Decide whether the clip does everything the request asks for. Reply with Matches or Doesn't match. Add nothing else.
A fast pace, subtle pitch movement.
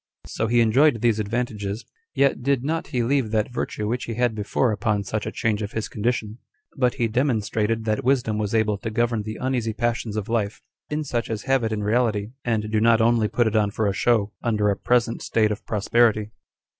Matches